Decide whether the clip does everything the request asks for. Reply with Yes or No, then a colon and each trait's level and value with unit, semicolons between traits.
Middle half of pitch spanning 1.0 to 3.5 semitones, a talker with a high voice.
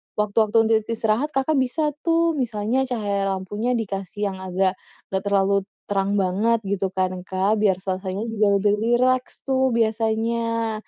Yes: average, 3.1 semitones; high, 215 Hz